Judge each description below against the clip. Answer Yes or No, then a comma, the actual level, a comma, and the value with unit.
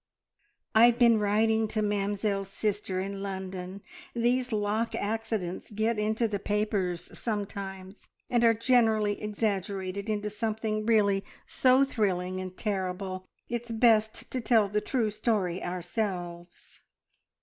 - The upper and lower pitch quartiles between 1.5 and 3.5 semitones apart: Yes, narrow, 2.5 semitones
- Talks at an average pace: No, slow, 120 wpm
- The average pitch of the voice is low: No, high, 210 Hz